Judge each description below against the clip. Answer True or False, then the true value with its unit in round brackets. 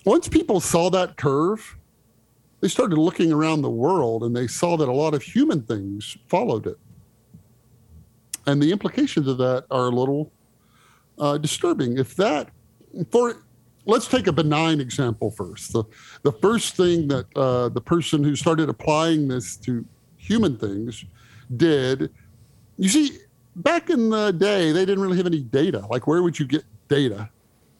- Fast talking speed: False (160 wpm)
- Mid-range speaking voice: True (145 Hz)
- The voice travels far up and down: True (5.9 semitones)